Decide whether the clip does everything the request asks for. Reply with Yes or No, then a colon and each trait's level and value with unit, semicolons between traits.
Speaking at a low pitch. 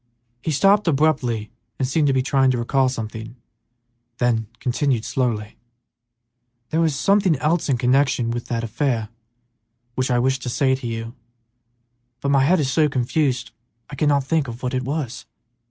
Yes: low, 130 Hz